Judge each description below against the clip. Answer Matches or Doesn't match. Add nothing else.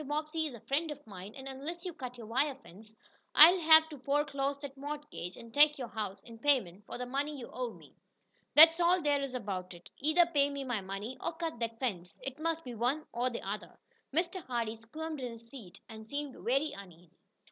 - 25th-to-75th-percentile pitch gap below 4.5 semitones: Doesn't match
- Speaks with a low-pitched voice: Doesn't match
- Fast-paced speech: Matches